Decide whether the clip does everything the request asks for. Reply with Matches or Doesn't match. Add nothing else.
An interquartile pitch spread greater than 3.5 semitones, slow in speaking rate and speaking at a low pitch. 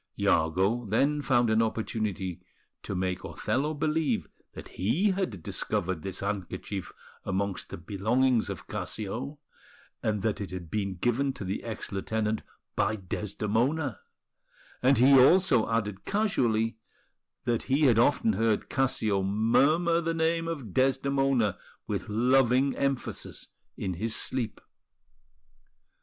Matches